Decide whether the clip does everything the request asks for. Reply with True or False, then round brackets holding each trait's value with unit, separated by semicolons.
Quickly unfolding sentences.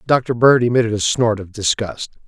False (185 wpm)